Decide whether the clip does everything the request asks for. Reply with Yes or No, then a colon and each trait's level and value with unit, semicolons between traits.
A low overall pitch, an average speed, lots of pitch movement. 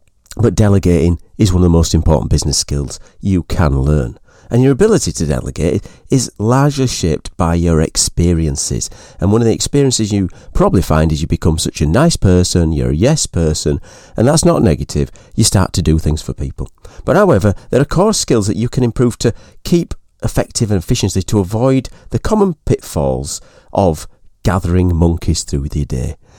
Yes: very low, 95 Hz; average, 180 wpm; wide, 6.1 semitones